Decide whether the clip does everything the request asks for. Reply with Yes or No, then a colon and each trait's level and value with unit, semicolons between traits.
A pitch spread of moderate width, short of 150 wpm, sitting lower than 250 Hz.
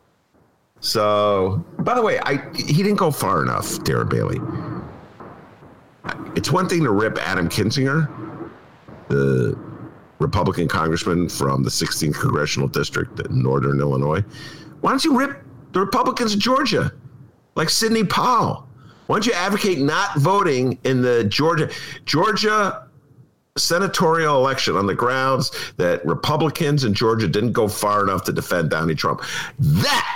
No: wide, 8.7 semitones; slow, 135 wpm; low, 135 Hz